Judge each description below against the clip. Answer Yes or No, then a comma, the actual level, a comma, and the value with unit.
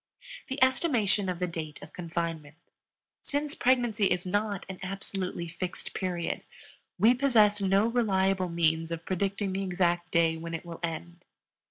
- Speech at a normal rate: Yes, average, 150 wpm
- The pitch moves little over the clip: No, average, 3.4 semitones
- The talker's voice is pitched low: No, medium, 185 Hz